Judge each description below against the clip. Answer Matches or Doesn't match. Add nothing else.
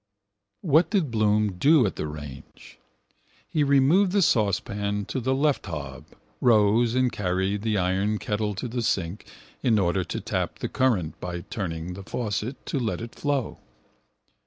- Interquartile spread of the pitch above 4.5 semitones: Matches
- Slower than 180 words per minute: Matches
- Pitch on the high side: Doesn't match